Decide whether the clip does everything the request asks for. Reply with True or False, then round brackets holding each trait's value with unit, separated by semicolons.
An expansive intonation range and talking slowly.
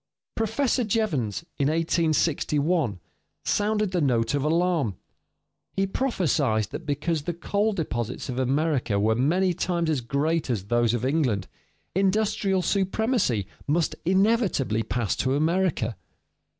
True (7.1 semitones; 125 wpm)